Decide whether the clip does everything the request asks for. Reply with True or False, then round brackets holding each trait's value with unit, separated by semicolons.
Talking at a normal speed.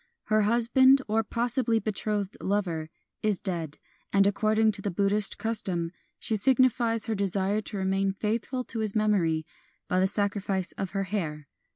True (160 wpm)